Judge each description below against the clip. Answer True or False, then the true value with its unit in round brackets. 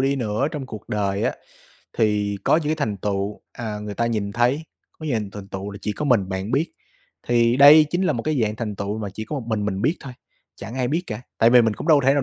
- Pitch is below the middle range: True (115 Hz)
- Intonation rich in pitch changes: False (4.7 semitones)